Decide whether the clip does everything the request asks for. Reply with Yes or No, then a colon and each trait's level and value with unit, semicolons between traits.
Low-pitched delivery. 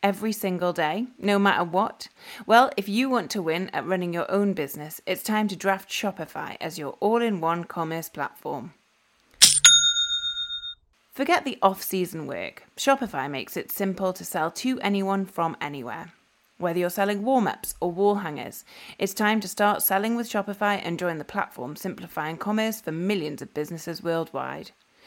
No: high, 195 Hz